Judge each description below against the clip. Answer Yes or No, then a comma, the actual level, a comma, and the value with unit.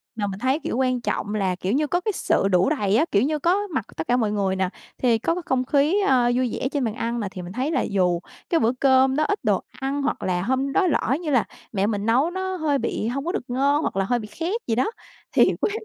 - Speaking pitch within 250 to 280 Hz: Yes, very high, 255 Hz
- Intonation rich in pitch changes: Yes, wide, 6.1 semitones